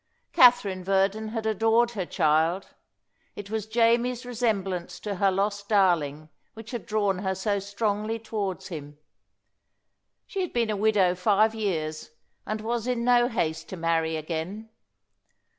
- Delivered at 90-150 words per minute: Yes, average, 140 wpm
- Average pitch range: Yes, average, 3.5 semitones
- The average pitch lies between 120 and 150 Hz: No, high, 205 Hz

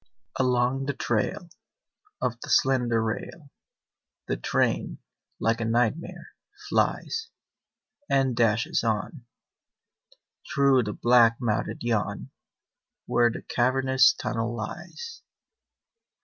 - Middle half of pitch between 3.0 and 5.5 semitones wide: No, narrow, 2.6 semitones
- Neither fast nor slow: No, slow, 95 wpm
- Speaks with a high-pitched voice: No, low, 120 Hz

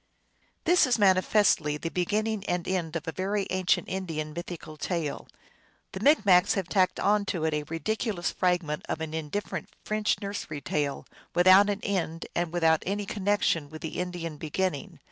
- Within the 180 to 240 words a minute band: No, average, 165 wpm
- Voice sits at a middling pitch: Yes, medium, 180 Hz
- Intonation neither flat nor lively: Yes, average, 3.9 semitones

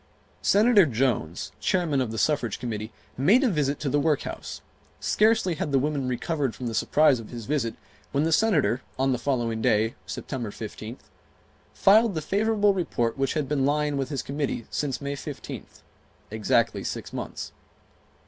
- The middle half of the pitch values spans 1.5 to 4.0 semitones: No, average, 4.9 semitones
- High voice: No, medium, 140 Hz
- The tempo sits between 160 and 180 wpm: Yes, average, 165 wpm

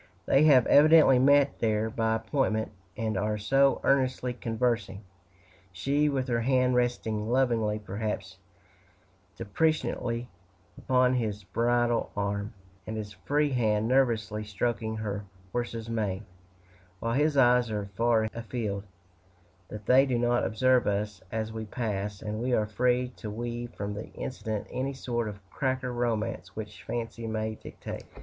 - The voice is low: Yes, low, 115 Hz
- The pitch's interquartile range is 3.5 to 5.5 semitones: No, average, 3.0 semitones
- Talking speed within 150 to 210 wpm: No, average, 140 wpm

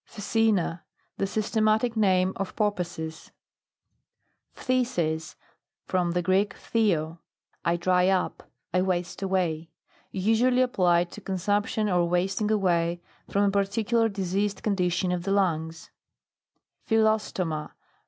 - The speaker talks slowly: Yes, slow, 115 wpm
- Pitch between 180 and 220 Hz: Yes, high, 190 Hz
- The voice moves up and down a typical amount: Yes, average, 3.4 semitones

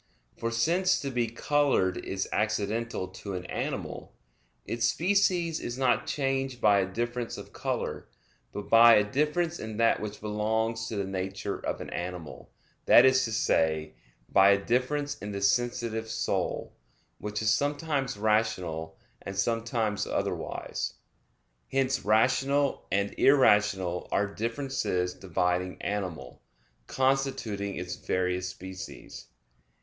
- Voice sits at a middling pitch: No, low, 110 Hz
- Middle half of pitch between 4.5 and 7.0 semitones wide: Yes, average, 5.1 semitones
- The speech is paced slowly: Yes, slow, 130 wpm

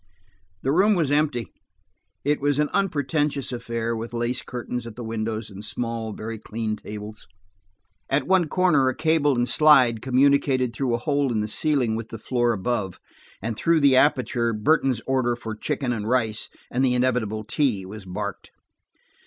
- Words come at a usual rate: Yes, average, 170 wpm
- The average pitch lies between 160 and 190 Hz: No, low, 120 Hz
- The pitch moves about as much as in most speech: Yes, average, 4.1 semitones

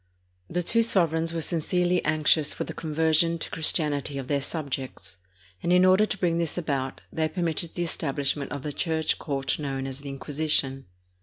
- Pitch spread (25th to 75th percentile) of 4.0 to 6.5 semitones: No, average, 3.2 semitones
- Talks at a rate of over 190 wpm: No, average, 175 wpm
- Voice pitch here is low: No, medium, 155 Hz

